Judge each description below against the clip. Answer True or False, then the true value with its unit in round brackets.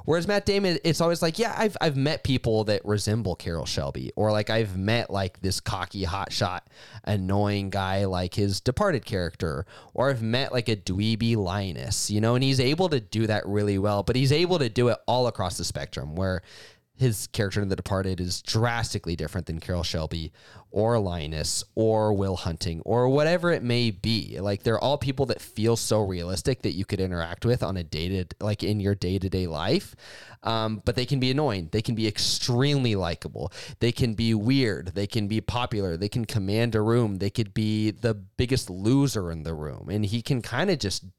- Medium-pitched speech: False (110 Hz)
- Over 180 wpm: True (200 wpm)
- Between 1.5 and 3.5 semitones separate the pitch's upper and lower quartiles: False (4.3 semitones)